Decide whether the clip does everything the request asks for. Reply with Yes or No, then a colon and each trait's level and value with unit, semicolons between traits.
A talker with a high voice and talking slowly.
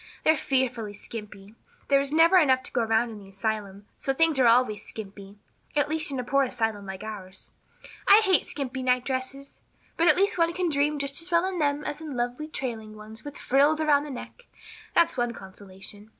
No: very high, 260 Hz; average, 195 wpm